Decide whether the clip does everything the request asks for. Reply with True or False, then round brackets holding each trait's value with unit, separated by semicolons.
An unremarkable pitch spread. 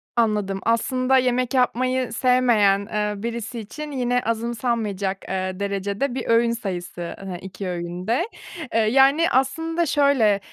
True (4.2 semitones)